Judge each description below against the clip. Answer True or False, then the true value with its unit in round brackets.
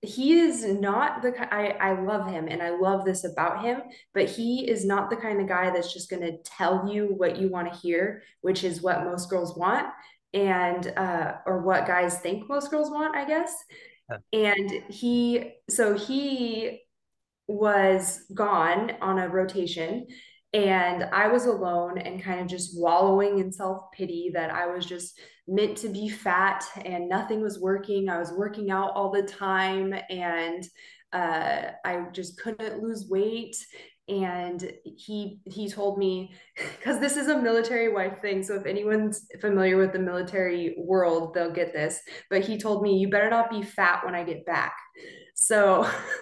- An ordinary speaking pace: True (175 wpm)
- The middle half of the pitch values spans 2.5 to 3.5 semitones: True (2.9 semitones)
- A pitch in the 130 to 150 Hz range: False (195 Hz)